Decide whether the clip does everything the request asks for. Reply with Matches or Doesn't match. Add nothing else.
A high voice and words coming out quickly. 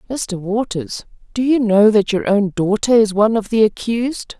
Doesn't match